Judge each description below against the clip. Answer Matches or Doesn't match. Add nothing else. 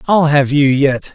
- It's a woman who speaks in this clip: Doesn't match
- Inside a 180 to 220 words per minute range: Matches